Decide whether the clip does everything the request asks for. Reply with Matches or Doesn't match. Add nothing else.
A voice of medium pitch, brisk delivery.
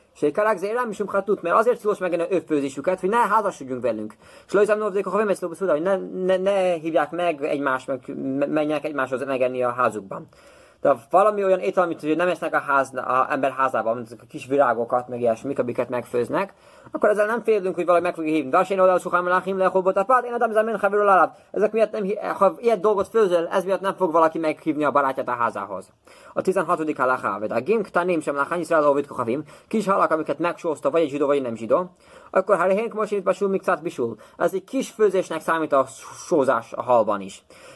Matches